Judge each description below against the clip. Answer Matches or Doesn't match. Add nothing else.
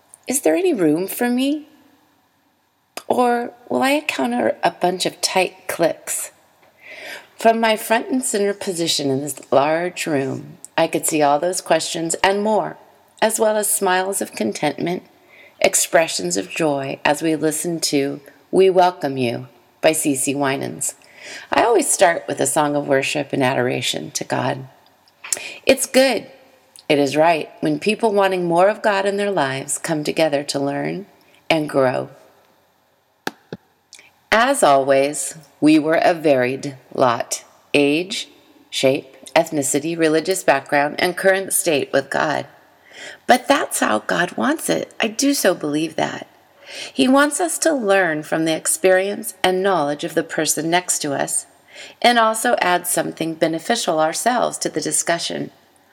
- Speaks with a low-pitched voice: Doesn't match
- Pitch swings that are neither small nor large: Doesn't match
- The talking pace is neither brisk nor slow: Matches